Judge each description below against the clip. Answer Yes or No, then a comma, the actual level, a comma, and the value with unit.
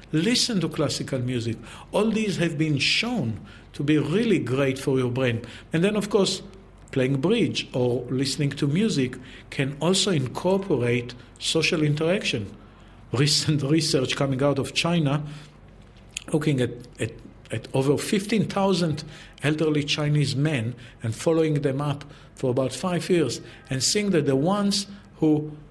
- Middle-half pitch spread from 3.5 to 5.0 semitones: Yes, average, 4.6 semitones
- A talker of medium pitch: Yes, medium, 145 Hz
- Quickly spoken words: No, average, 140 wpm